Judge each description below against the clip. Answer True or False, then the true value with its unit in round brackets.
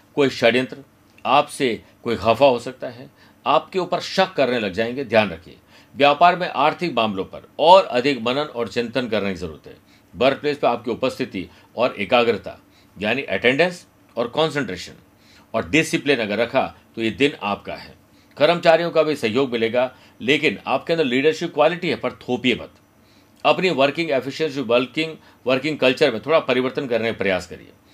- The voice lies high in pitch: False (130 Hz)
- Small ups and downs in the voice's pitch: False (5.3 semitones)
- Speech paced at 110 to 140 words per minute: False (165 wpm)